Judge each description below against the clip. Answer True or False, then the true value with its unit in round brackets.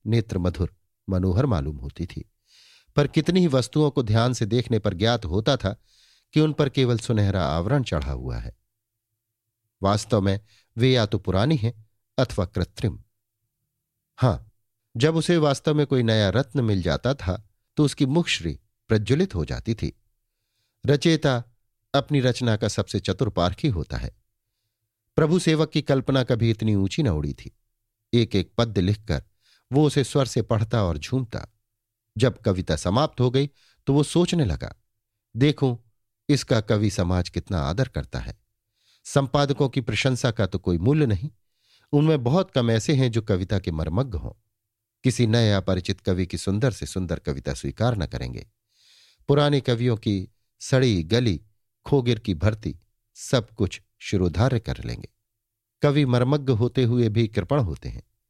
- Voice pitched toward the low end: True (110 Hz)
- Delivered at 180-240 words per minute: False (155 wpm)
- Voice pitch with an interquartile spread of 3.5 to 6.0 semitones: True (4.2 semitones)